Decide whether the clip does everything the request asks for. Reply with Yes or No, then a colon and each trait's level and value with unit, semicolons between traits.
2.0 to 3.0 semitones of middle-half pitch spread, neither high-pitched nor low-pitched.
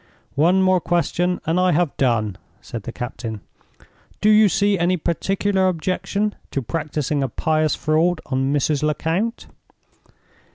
No: average, 4.7 semitones; medium, 165 Hz